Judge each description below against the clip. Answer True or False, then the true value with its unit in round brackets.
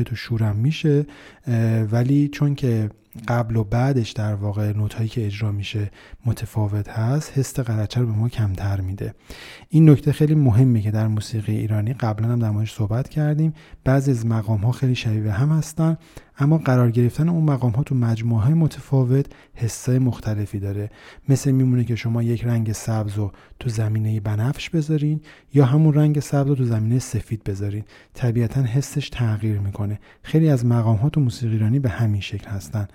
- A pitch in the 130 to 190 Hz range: False (115 Hz)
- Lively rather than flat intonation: False (4.1 semitones)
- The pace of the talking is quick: True (170 wpm)